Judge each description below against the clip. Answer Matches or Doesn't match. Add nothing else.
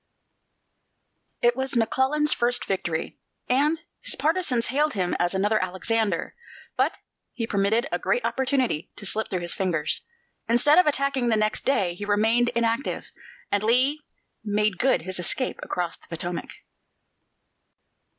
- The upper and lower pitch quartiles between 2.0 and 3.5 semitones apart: Doesn't match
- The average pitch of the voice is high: Matches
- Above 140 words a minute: Doesn't match